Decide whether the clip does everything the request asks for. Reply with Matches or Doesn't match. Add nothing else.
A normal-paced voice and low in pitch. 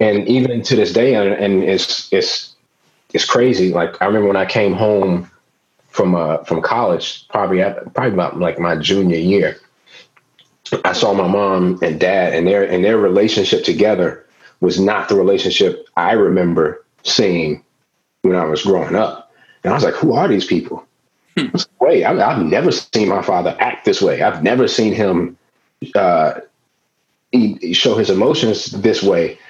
Matches